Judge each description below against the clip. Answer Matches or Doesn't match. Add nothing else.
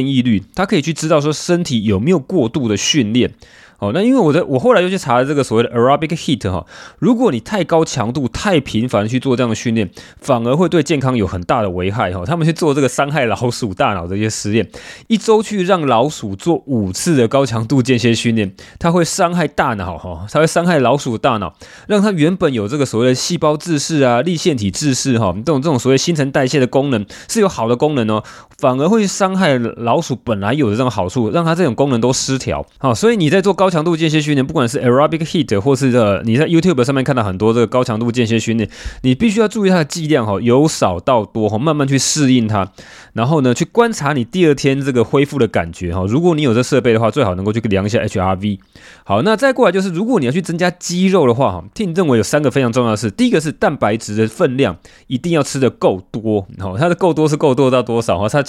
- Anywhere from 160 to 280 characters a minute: Doesn't match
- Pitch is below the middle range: Matches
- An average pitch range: Doesn't match